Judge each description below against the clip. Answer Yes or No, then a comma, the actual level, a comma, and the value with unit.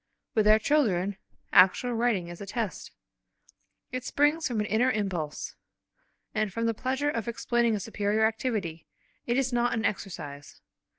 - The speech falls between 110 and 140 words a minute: No, average, 155 wpm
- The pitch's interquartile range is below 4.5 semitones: Yes, average, 3.7 semitones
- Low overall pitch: No, high, 220 Hz